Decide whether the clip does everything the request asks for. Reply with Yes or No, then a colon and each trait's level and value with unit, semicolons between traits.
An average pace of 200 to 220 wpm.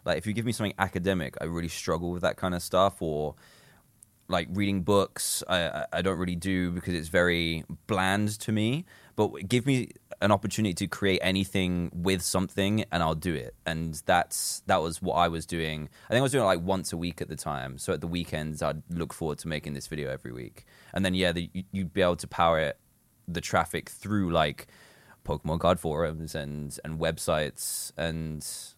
Yes: fast, 205 wpm